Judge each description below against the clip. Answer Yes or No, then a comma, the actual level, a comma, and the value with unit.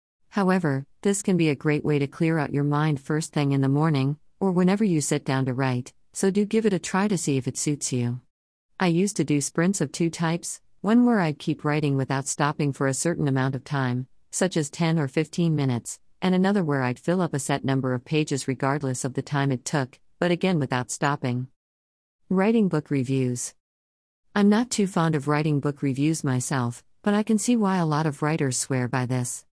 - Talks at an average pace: No, fast, 220 wpm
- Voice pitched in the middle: Yes, medium, 150 Hz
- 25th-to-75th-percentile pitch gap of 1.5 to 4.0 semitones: No, average, 4.4 semitones